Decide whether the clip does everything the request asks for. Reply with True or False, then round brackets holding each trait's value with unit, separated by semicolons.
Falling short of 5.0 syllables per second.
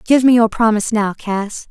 False (5.1 syllables/s)